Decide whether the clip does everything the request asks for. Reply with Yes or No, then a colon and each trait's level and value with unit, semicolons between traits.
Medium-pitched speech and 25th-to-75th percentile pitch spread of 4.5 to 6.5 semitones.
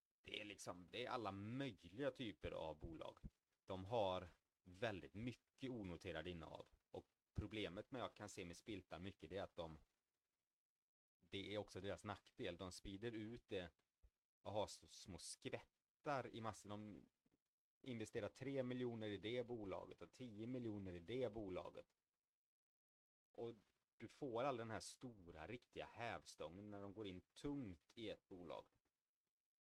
No: low, 105 Hz; average, 4.9 semitones